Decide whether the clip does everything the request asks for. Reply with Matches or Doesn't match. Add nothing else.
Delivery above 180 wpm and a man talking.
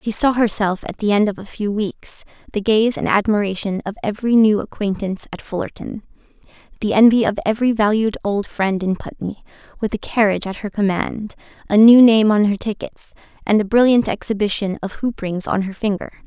Doesn't match